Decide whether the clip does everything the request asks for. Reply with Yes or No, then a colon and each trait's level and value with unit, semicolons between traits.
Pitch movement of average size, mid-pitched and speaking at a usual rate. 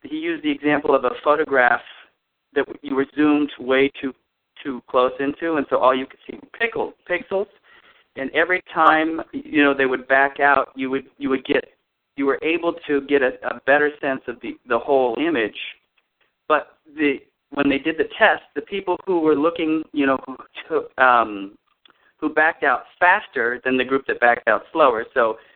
Yes: average, 4.1 semitones; medium, 145 Hz; average, 190 wpm